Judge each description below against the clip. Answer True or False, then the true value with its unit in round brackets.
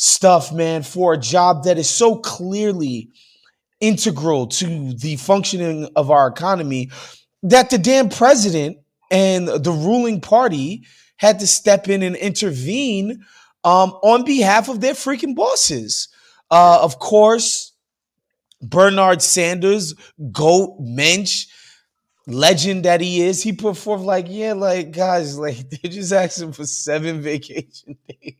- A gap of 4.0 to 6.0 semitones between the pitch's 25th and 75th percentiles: True (4.8 semitones)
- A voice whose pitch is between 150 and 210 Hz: True (185 Hz)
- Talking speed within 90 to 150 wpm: True (135 wpm)